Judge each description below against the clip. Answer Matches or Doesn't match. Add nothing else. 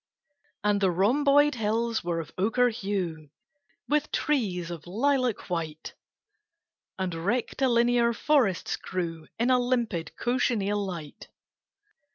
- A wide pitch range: Matches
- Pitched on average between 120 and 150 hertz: Doesn't match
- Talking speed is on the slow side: Matches